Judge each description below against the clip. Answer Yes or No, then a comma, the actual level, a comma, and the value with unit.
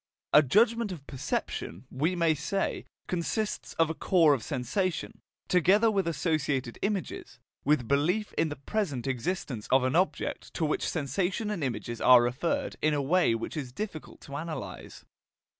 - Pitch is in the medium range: Yes, medium, 155 Hz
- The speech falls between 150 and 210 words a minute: Yes, average, 160 wpm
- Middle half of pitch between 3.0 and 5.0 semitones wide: No, wide, 5.6 semitones